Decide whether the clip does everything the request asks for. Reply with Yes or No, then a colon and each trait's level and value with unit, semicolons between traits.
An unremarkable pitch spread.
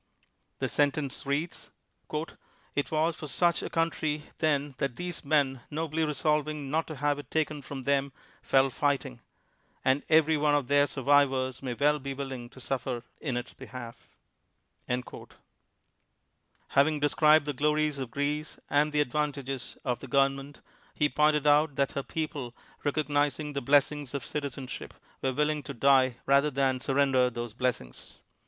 No: narrow, 2.1 semitones